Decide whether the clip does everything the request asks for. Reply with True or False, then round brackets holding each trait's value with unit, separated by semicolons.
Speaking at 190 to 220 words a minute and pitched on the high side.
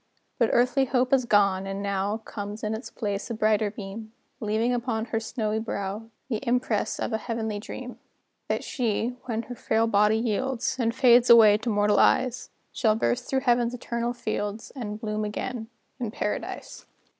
False (170 wpm; 225 Hz)